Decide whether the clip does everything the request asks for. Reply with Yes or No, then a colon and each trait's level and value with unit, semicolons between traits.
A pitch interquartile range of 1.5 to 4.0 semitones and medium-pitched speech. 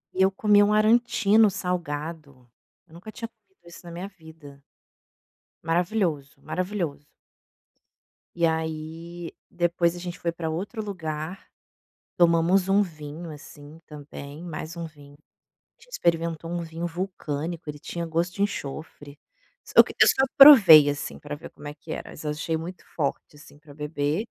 Yes: average, 3.3 semitones; medium, 165 Hz